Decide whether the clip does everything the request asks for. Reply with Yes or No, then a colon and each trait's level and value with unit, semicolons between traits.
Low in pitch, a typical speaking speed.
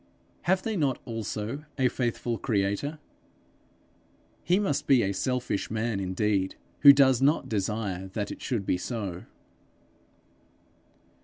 No: low, 115 Hz; slow, 125 wpm